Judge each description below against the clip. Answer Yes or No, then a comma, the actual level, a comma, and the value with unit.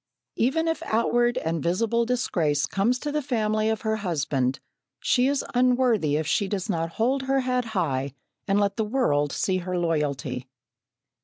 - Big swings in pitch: Yes, wide, 7.2 semitones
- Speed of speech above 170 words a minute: No, average, 165 wpm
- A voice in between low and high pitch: No, high, 210 Hz